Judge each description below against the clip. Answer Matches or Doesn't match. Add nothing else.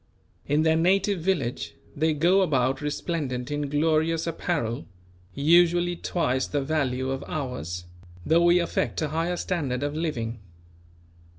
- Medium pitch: Matches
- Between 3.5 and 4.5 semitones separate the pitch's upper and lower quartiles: Matches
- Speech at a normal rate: Doesn't match